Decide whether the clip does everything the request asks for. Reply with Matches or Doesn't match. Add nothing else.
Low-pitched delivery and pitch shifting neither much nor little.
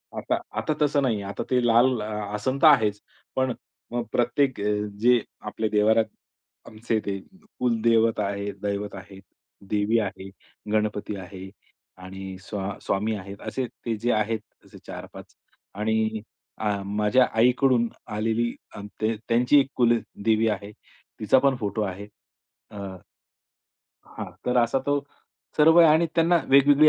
Matches